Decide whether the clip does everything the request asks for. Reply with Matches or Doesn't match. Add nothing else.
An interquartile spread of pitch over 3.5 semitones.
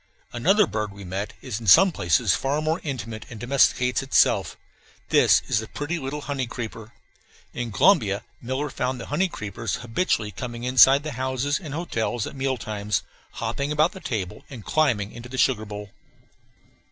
Matches